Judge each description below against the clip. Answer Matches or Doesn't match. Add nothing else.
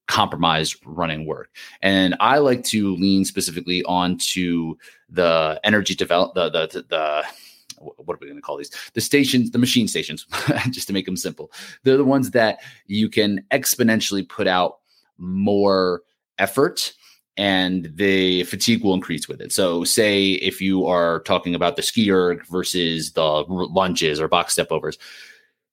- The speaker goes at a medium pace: Matches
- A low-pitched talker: Matches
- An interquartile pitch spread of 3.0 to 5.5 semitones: Doesn't match